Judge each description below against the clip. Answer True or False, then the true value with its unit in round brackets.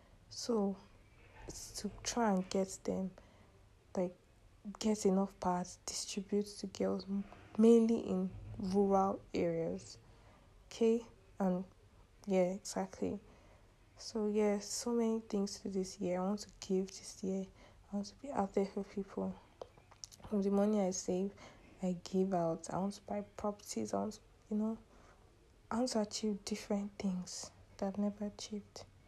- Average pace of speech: True (150 wpm)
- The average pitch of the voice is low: False (190 Hz)